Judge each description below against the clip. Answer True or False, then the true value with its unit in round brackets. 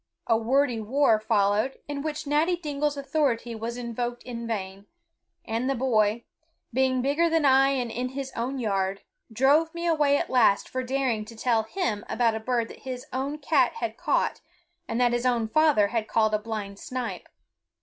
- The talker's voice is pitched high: True (245 Hz)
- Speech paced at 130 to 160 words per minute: False (180 wpm)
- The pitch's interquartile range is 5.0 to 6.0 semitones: False (3.9 semitones)